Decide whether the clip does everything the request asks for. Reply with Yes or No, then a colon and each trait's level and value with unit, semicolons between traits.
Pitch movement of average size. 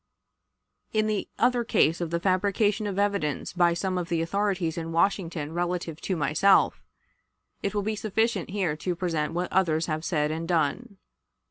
Yes: average, 3.6 semitones